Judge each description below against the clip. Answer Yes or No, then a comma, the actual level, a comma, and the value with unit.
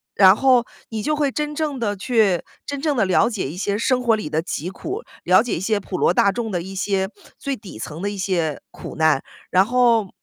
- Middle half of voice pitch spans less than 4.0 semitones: No, average, 5.1 semitones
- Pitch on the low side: No, high, 205 Hz